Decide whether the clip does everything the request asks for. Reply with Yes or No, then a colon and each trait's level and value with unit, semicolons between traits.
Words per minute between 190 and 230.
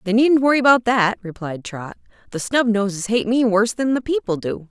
Yes: fast, 205 wpm